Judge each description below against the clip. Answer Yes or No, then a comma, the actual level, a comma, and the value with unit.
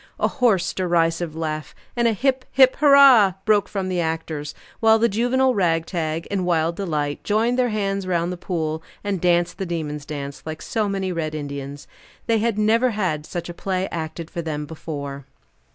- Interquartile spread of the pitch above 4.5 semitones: Yes, average, 5.1 semitones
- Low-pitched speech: No, medium, 175 Hz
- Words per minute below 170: No, average, 180 wpm